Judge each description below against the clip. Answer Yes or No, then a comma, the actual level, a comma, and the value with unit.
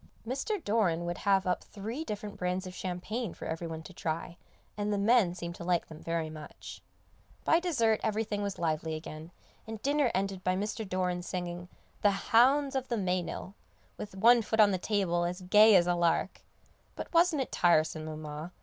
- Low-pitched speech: No, medium, 185 Hz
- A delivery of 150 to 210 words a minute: Yes, average, 185 wpm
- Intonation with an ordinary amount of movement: Yes, average, 4.2 semitones